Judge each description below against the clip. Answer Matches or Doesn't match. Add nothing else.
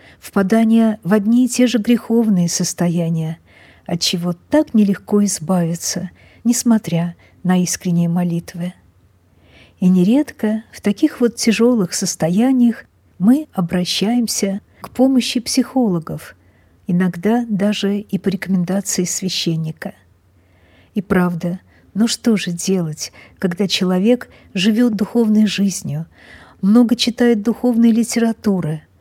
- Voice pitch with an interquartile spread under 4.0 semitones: Doesn't match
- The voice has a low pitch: Doesn't match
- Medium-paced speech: Doesn't match